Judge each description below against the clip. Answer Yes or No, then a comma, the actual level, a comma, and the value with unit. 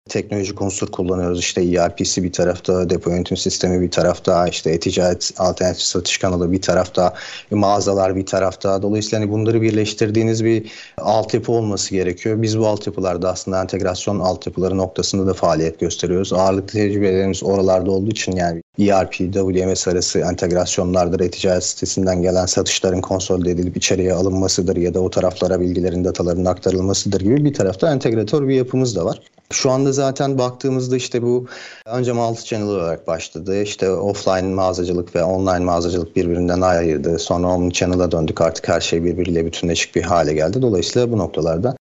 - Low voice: Yes, very low, 95 Hz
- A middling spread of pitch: No, narrow, 2.3 semitones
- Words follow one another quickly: Yes, fast, 155 wpm